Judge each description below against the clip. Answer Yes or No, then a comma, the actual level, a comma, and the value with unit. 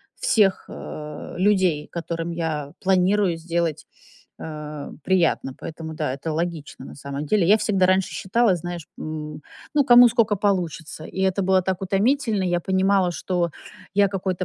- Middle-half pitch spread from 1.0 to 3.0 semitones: No, average, 3.4 semitones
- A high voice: No, medium, 180 Hz